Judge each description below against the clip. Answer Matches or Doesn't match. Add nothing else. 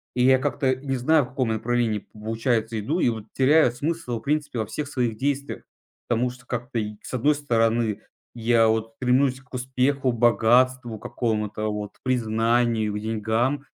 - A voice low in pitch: Matches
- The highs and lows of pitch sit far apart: Doesn't match